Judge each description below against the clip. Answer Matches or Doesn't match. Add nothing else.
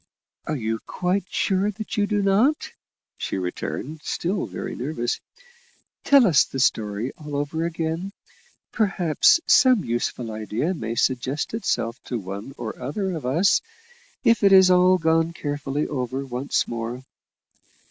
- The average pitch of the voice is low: Doesn't match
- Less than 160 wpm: Matches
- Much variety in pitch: Matches